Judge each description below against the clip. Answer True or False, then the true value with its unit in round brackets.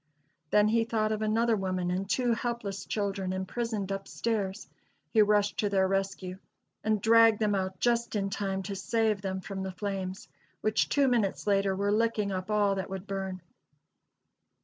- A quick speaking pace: False (170 wpm)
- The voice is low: False (200 Hz)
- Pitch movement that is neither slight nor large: False (2.2 semitones)